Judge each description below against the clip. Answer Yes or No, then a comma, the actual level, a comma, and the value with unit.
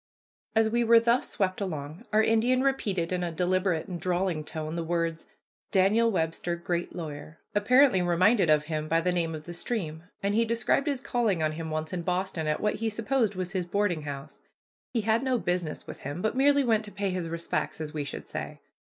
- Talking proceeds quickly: Yes, fast, 210 wpm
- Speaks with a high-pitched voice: No, medium, 180 Hz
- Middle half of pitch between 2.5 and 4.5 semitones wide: No, average, 5.2 semitones